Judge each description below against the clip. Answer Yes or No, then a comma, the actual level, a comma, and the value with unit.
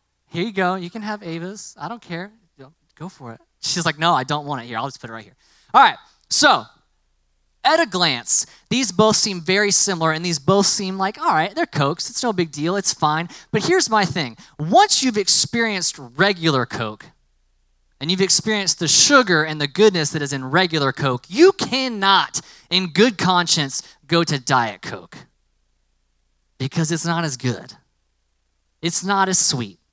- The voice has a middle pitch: Yes, medium, 165 Hz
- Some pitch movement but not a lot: No, wide, 7.5 semitones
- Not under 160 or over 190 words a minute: Yes, average, 185 wpm